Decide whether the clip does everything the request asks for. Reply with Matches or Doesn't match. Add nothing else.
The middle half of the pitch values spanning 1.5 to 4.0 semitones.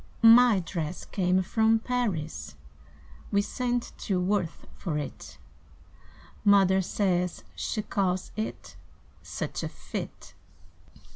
Matches